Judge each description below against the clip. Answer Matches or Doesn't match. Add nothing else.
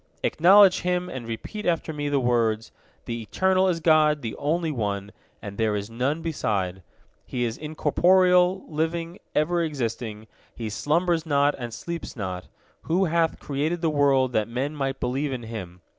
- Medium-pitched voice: Matches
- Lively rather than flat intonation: Matches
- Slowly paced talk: Doesn't match